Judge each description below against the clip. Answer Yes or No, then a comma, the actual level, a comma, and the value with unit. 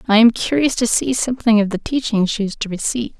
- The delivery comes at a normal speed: No, fast, 245 wpm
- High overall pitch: Yes, high, 225 Hz